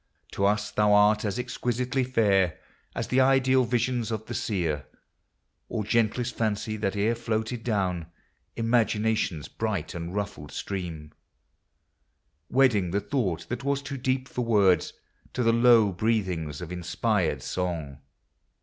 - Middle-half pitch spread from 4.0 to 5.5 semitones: Yes, average, 4.6 semitones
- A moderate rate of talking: No, slow, 130 wpm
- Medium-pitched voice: No, low, 110 Hz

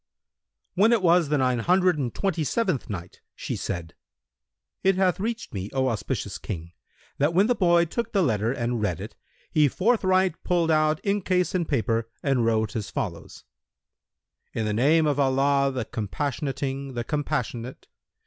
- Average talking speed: Yes, average, 160 wpm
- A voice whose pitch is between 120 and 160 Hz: Yes, medium, 140 Hz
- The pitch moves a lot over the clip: Yes, wide, 7.2 semitones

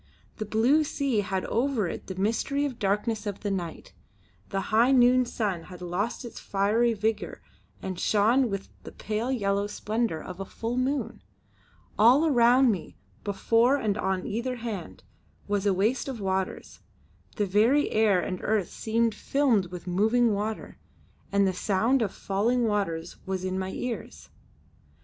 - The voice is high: Yes, high, 215 Hz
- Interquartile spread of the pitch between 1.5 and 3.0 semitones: No, average, 3.7 semitones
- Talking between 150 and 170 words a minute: Yes, average, 160 wpm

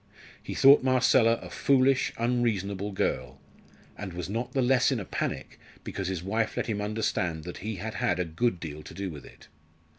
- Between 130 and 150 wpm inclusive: No, average, 190 wpm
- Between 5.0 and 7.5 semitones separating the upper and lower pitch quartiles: Yes, average, 5.3 semitones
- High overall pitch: No, low, 105 Hz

